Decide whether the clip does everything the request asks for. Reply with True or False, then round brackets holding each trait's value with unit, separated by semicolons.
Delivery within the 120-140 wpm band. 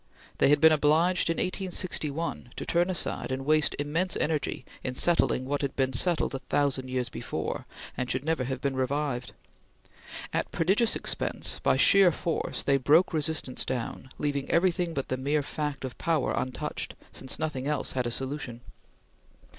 False (165 wpm)